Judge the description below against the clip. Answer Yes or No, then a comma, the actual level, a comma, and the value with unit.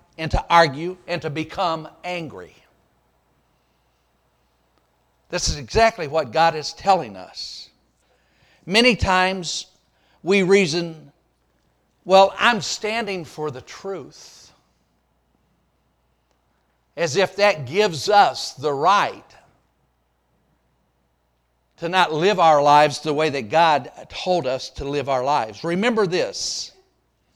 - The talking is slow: Yes, slow, 105 wpm